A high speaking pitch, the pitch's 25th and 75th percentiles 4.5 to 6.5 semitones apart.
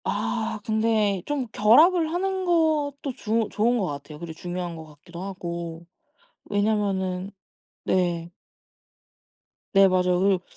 Yes: high, 200 Hz; average, 5.1 semitones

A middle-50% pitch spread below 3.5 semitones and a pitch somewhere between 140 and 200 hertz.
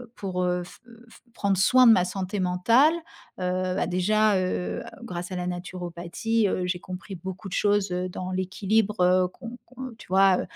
Yes: narrow, 2.4 semitones; medium, 185 Hz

